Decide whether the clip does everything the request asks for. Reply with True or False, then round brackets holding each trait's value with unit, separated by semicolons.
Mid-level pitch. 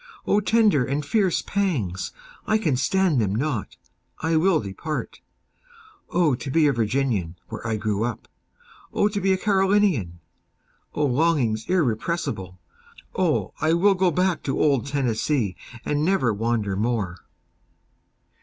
True (145 Hz)